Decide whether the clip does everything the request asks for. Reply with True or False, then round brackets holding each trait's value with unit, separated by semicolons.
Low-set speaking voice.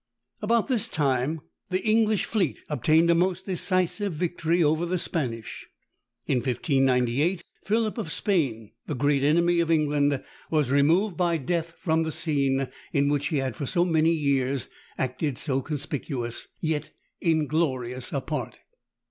False (155 Hz)